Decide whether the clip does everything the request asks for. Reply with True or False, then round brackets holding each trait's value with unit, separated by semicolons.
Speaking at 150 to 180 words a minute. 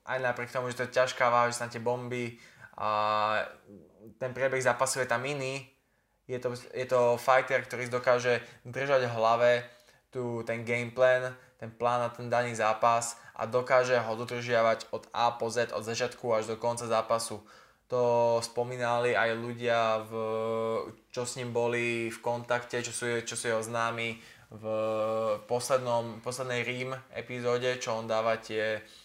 True (165 wpm)